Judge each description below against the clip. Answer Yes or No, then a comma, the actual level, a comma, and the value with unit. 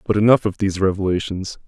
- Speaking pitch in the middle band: No, low, 100 Hz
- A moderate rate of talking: Yes, average, 180 wpm